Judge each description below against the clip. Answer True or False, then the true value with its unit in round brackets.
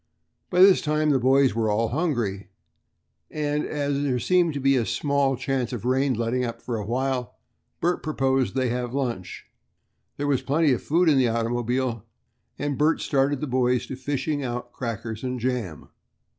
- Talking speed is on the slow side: False (185 wpm)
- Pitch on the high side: False (130 Hz)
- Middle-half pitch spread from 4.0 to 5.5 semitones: False (3.1 semitones)